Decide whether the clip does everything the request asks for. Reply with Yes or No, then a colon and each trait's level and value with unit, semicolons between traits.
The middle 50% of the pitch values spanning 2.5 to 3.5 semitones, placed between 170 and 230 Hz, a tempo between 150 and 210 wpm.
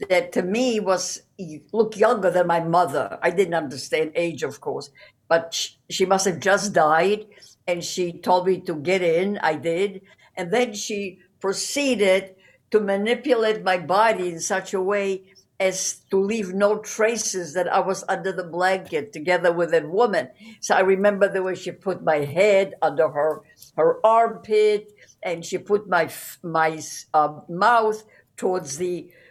Yes: average, 3.1 semitones; high, 190 Hz; average, 165 wpm